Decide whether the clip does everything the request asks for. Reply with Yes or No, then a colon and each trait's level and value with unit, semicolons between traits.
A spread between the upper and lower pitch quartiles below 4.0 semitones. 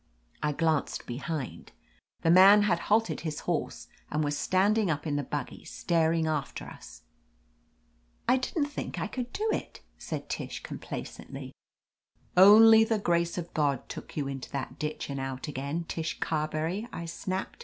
No: average, 4.9 semitones